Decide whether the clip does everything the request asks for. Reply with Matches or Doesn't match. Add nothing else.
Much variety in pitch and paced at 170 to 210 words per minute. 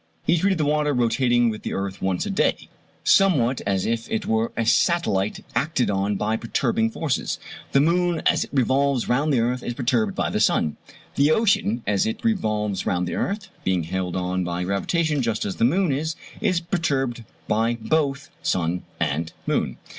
Matches